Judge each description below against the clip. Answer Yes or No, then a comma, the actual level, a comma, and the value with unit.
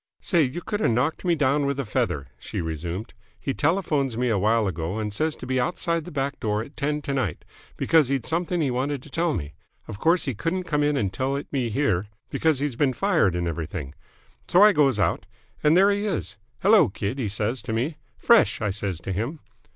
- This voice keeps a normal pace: No, fast, 220 wpm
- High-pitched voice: No, low, 135 Hz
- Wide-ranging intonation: Yes, wide, 7.0 semitones